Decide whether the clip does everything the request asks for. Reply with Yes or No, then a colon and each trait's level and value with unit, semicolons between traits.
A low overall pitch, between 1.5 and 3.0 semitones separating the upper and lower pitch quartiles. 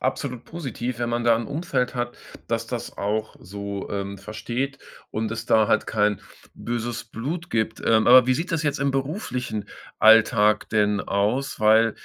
No: low, 115 Hz; average, 3.4 semitones